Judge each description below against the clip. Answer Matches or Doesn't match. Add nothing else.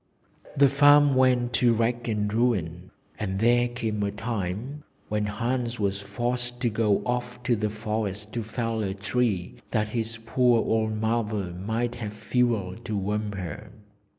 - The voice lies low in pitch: Matches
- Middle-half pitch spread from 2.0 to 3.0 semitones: Matches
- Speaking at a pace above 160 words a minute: Doesn't match